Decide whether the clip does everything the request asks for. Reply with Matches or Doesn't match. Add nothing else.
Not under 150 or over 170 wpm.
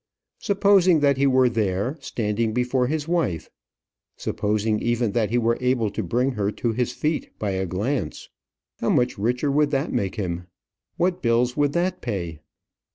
Matches